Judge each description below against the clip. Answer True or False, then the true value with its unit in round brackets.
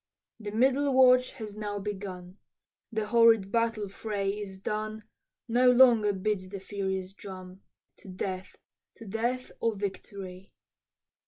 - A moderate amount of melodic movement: True (3.0 semitones)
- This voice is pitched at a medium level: False (210 Hz)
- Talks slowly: True (130 wpm)